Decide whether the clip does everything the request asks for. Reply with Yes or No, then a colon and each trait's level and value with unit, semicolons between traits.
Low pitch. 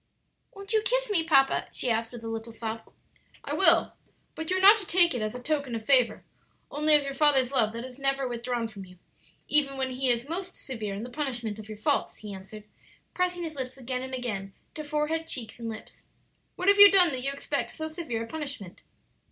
No: very high, 260 Hz